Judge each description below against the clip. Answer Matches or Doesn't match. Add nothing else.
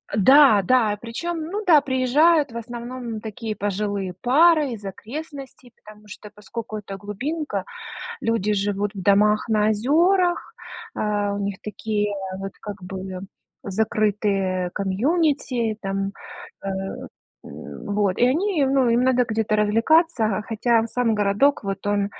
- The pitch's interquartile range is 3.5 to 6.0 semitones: Matches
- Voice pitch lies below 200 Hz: Doesn't match